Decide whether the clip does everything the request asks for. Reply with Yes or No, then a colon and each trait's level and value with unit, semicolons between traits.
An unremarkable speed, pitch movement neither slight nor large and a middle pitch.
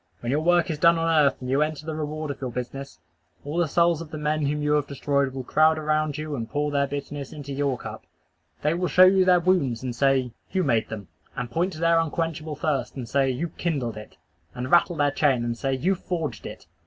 No: fast, 240 wpm; average, 3.3 semitones; medium, 150 Hz